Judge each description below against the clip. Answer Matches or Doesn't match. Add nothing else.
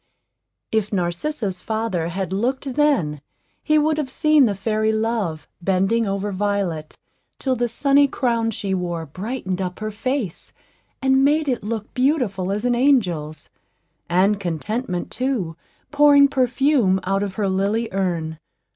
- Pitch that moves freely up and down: Matches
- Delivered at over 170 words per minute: Doesn't match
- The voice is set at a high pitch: Matches